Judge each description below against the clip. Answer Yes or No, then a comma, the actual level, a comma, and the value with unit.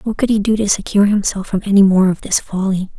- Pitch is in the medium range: No, high, 200 Hz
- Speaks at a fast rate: Yes, fast, 260 wpm